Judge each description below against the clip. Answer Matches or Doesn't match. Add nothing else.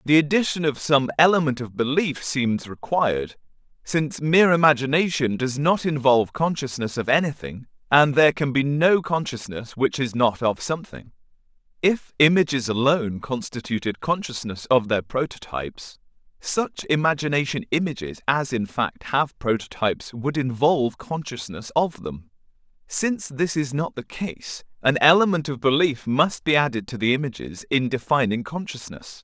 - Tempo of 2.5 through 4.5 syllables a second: Doesn't match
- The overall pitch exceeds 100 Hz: Matches